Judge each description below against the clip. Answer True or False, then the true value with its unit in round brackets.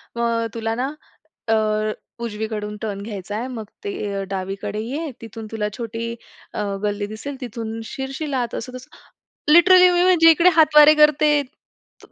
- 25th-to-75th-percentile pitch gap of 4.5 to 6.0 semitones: True (5.6 semitones)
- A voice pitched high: True (230 Hz)